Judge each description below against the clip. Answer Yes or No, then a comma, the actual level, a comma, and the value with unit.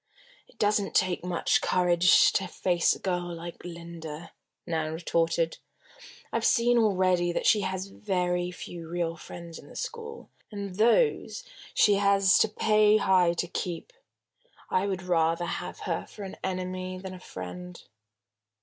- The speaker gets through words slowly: No, average, 150 wpm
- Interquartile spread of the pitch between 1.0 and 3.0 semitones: Yes, narrow, 2.5 semitones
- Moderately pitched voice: Yes, medium, 180 Hz